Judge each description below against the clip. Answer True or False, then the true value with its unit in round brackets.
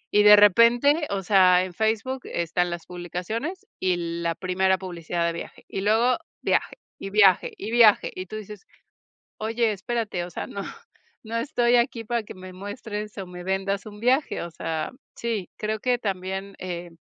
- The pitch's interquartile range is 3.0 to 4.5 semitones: True (3.8 semitones)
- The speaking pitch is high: True (200 Hz)